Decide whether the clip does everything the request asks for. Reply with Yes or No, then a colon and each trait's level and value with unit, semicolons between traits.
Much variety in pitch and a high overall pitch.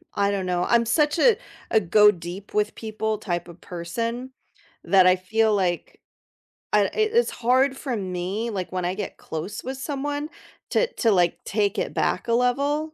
Yes: wide, 5.8 semitones; high, 215 Hz